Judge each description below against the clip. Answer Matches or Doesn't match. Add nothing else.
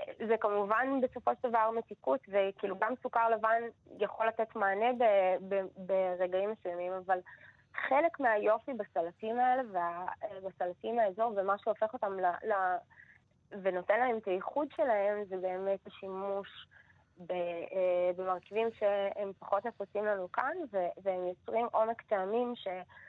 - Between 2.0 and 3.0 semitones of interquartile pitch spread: Doesn't match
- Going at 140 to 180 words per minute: Doesn't match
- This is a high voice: Matches